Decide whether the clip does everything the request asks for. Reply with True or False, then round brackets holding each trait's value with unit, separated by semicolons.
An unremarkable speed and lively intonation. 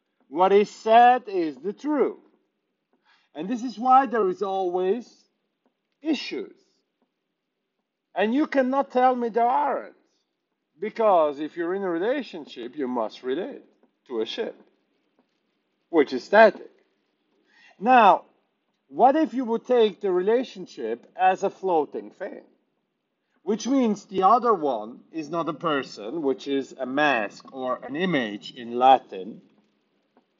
False (130 wpm; 6.9 semitones)